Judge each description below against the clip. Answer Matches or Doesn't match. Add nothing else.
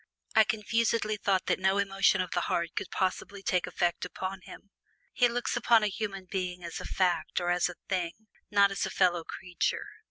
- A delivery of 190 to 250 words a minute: Matches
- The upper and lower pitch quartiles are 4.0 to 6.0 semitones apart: Doesn't match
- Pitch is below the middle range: Doesn't match